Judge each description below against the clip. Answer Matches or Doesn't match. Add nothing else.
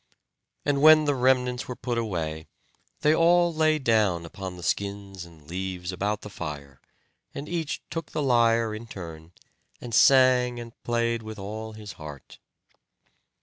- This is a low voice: Matches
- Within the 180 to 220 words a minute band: Doesn't match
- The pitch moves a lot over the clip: Matches